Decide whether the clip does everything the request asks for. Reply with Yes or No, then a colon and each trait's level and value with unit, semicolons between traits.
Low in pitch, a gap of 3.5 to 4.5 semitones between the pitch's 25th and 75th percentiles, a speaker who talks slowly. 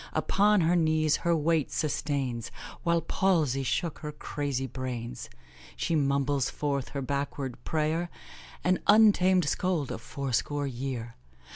No: medium, 145 Hz; average, 3.9 semitones; slow, 125 wpm